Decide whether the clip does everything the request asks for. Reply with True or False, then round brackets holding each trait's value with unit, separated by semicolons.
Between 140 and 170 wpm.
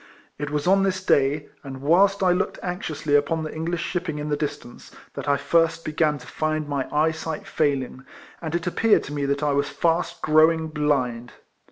False (190 wpm)